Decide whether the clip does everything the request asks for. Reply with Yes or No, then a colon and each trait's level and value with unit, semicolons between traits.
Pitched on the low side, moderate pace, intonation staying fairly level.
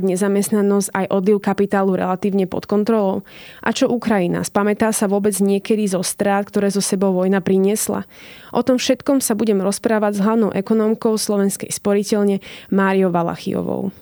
No: high, 200 Hz; average, 145 wpm; narrow, 1.9 semitones